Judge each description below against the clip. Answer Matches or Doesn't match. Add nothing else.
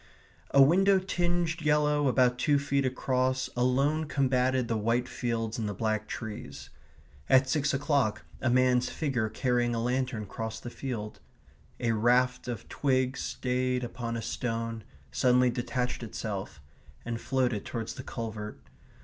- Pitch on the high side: Doesn't match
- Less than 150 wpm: Matches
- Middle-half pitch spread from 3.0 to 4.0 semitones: Doesn't match